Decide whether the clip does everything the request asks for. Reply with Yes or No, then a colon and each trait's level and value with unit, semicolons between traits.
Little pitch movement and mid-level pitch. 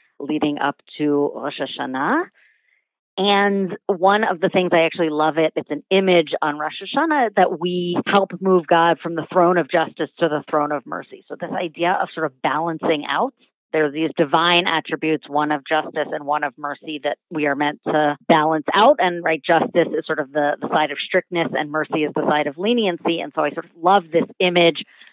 No: average, 3.2 semitones; medium, 165 Hz